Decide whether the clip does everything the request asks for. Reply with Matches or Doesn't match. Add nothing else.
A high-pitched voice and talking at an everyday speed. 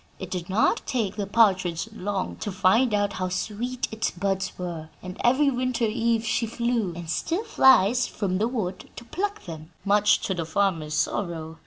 Matches